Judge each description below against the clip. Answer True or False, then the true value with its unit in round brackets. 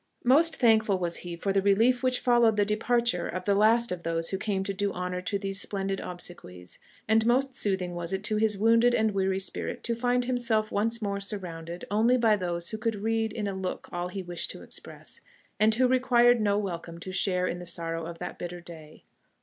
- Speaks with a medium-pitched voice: False (200 Hz)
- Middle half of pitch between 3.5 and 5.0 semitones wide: True (4.0 semitones)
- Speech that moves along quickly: True (215 wpm)